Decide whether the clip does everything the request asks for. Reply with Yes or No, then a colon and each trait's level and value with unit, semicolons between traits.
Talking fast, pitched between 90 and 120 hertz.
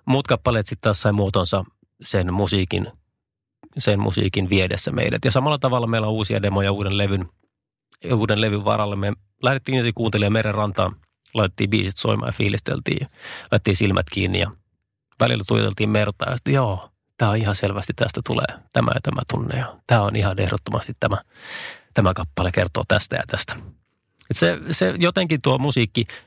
Yes: fast, 165 wpm; low, 105 Hz